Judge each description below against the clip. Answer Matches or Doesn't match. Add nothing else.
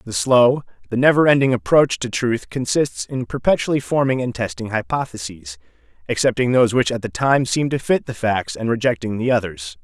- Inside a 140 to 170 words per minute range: Doesn't match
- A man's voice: Matches